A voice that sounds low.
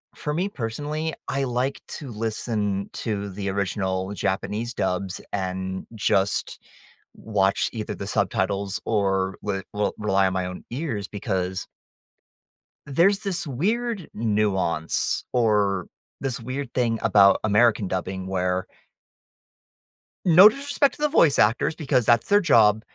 Yes: low, 105 Hz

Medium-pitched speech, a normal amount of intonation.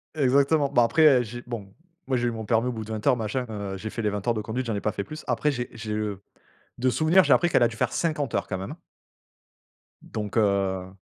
No: low, 115 Hz; average, 3.6 semitones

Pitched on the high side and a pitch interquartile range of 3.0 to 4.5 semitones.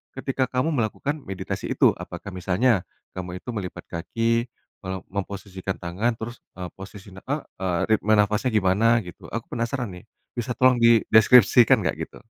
No: low, 110 Hz; average, 4.2 semitones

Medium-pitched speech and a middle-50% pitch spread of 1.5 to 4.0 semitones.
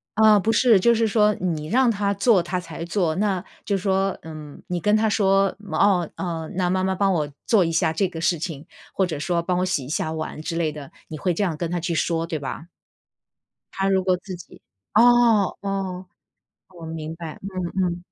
Yes: medium, 180 Hz; average, 3.3 semitones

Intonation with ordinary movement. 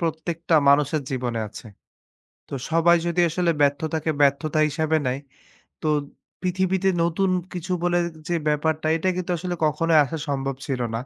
Yes: average, 3.2 semitones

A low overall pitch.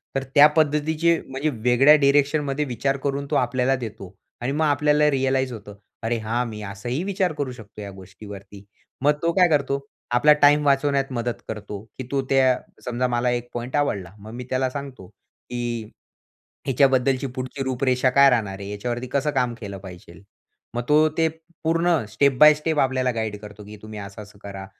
Yes: low, 130 Hz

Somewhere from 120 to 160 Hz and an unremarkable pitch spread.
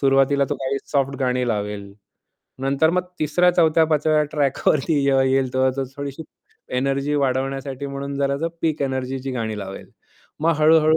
No: medium, 140 Hz; narrow, 2.3 semitones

